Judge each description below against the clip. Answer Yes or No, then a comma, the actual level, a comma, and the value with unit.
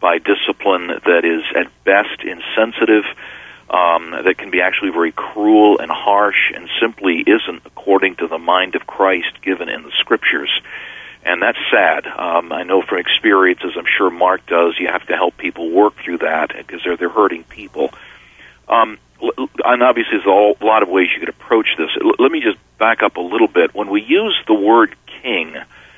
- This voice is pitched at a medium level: No, low, 110 Hz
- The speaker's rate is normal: Yes, average, 185 wpm